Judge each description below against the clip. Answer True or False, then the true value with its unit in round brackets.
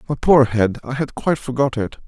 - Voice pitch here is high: False (130 Hz)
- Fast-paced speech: True (230 wpm)